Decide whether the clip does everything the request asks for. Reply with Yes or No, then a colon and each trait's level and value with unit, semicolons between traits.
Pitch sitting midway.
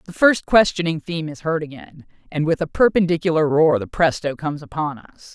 Yes: medium, 160 Hz